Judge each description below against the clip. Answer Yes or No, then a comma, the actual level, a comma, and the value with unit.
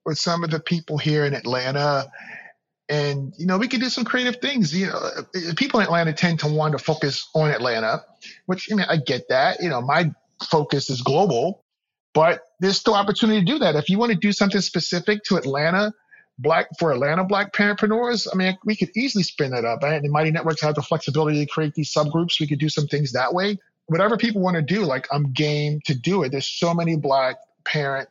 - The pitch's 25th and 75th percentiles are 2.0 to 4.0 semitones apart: No, average, 5.0 semitones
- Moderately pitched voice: Yes, medium, 165 Hz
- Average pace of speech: No, fast, 225 wpm